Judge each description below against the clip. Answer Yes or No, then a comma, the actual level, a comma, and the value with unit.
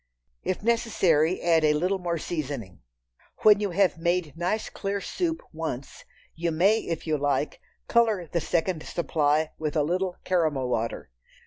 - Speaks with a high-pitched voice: No, medium, 170 Hz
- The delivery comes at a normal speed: Yes, average, 150 wpm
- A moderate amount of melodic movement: Yes, average, 3.7 semitones